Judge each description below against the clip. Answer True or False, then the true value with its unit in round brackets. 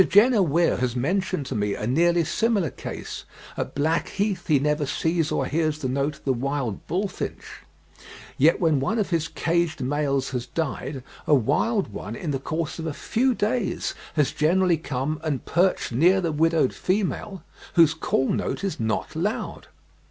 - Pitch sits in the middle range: True (160 Hz)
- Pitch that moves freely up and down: False (4.7 semitones)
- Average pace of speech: True (170 wpm)